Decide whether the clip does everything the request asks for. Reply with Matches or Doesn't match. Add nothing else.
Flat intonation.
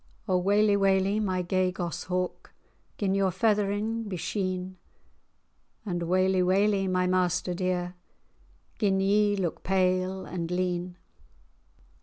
Matches